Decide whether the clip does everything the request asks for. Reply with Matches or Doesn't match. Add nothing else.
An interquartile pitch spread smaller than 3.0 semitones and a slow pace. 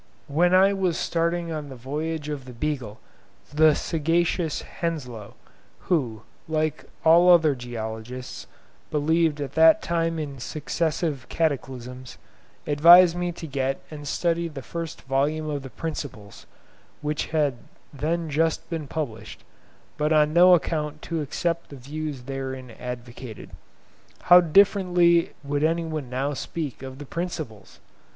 Doesn't match